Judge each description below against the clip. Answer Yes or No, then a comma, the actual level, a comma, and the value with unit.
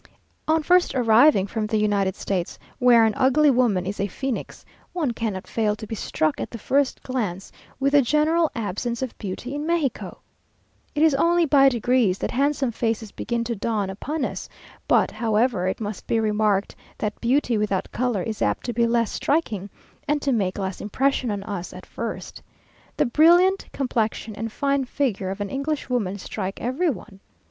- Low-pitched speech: No, high, 230 Hz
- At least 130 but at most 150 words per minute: No, average, 180 wpm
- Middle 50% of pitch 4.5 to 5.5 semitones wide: Yes, average, 5.0 semitones